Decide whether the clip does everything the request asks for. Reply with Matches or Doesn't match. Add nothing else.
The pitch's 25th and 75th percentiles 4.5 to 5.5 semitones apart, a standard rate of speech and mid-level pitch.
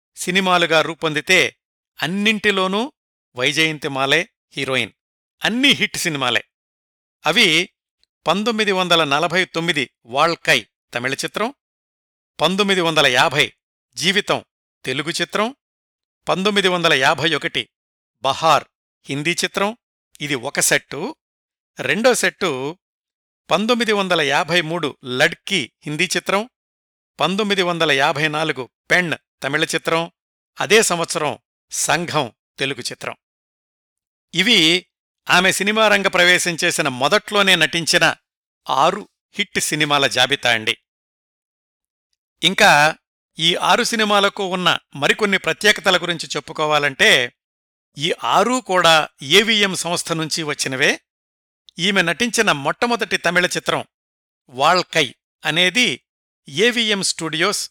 Matches